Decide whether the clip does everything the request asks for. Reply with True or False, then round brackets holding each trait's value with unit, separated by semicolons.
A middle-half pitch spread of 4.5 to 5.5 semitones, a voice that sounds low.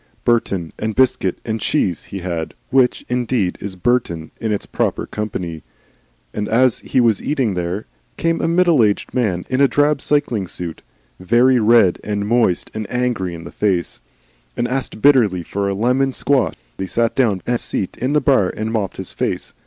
True (5.1 semitones; 110 Hz)